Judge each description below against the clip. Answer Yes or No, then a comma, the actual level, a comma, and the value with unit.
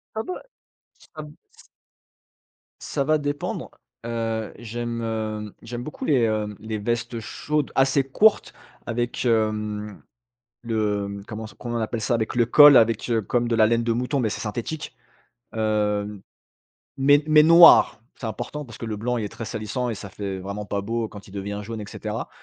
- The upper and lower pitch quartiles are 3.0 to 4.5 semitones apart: No, narrow, 2.6 semitones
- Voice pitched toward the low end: Yes, low, 115 Hz